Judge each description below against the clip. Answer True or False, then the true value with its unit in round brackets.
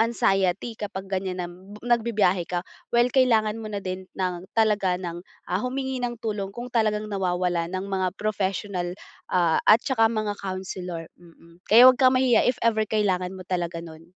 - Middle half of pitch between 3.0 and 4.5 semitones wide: True (3.7 semitones)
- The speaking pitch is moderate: False (195 Hz)